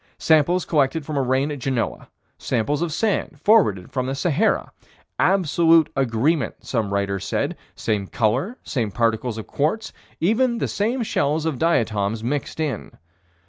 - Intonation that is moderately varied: No, wide, 6.3 semitones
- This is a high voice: No, medium, 140 Hz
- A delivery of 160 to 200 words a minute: No, average, 145 wpm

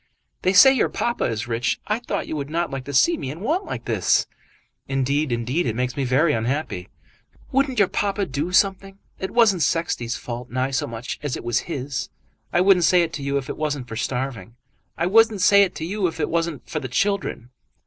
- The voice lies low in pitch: No, medium, 155 Hz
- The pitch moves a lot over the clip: Yes, wide, 7.2 semitones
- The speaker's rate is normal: No, fast, 220 wpm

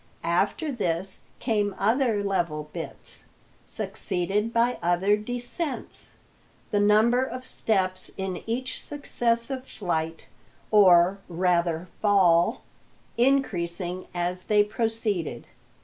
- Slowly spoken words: Yes, slow, 95 wpm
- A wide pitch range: No, average, 4.8 semitones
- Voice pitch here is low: No, high, 200 Hz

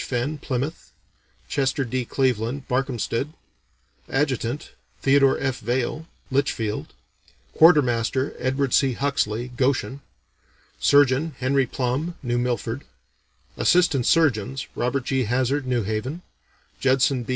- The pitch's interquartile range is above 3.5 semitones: No, narrow, 2.4 semitones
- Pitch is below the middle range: Yes, low, 130 Hz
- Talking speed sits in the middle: No, slow, 105 wpm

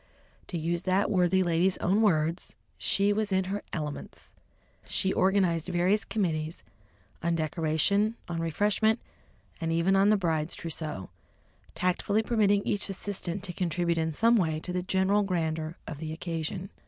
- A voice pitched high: No, medium, 180 Hz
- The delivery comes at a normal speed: Yes, average, 150 wpm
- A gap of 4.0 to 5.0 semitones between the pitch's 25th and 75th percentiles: No, average, 3.4 semitones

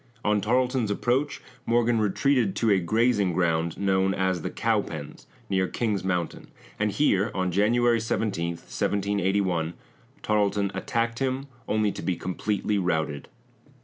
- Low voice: Yes, low, 100 Hz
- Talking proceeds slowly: Yes, slow, 130 wpm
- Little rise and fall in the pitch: No, average, 3.7 semitones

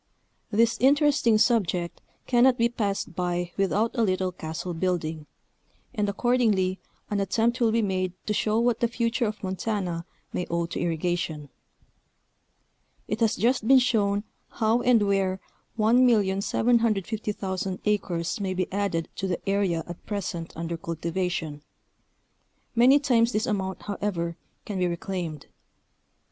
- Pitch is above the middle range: Yes, high, 200 Hz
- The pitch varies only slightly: No, average, 4.3 semitones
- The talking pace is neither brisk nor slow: No, slow, 130 wpm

